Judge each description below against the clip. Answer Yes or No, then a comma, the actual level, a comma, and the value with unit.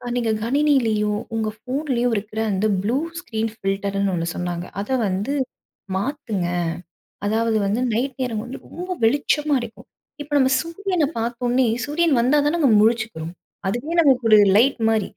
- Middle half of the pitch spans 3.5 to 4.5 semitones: No, average, 4.9 semitones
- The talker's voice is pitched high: Yes, high, 235 Hz